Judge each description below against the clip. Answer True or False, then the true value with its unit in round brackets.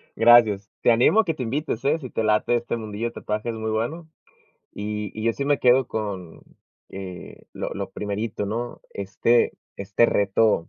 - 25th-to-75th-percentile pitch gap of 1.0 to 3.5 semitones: True (2.7 semitones)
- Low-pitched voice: True (110 Hz)